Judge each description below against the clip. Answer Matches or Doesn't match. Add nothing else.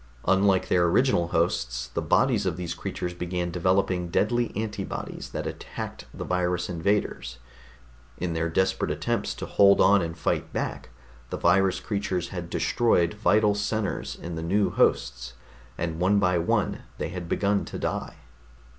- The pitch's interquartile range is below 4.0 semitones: Matches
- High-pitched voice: Doesn't match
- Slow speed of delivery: Doesn't match